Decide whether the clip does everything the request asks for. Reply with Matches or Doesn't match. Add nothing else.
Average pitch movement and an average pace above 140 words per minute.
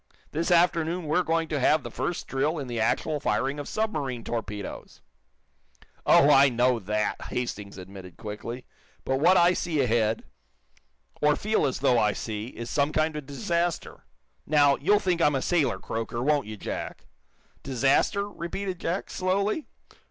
Doesn't match